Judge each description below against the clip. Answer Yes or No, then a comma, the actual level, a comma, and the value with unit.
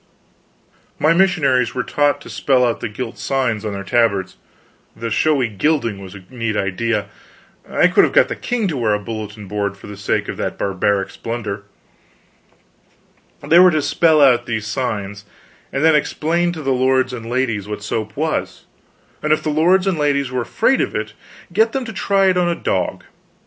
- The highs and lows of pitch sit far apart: Yes, wide, 6.5 semitones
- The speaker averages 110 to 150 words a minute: No, average, 190 wpm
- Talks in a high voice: No, low, 125 Hz